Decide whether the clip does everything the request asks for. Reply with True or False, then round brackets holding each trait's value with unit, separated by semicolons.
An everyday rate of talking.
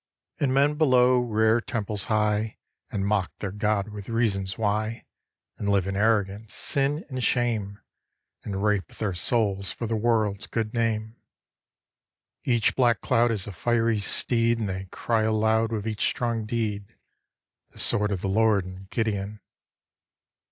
True (150 wpm)